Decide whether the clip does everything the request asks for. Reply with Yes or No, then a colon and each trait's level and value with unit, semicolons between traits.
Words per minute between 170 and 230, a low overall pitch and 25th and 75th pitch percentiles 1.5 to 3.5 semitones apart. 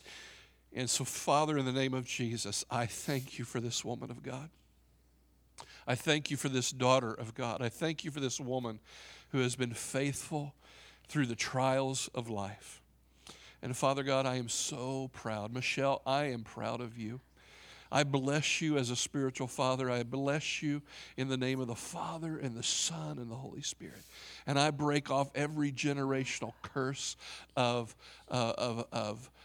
Yes: average, 175 wpm; low, 130 Hz; average, 2.9 semitones